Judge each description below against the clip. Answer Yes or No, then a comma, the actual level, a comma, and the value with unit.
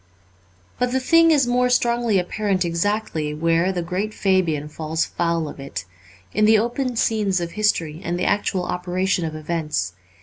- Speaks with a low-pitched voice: No, medium, 180 Hz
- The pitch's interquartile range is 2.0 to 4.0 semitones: No, average, 4.7 semitones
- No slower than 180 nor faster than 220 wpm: No, average, 170 wpm